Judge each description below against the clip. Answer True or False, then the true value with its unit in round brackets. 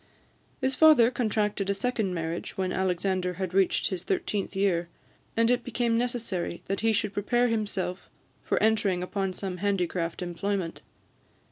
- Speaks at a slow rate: False (145 wpm)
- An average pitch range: True (3.6 semitones)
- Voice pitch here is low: False (195 Hz)